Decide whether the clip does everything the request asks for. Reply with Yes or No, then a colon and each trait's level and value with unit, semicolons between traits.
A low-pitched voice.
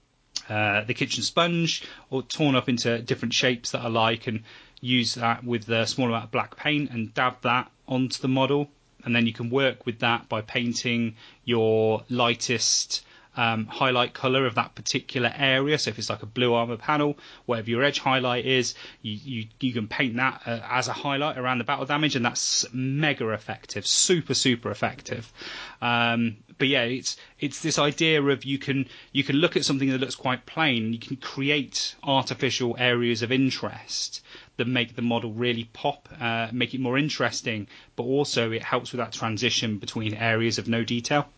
Yes: low, 125 Hz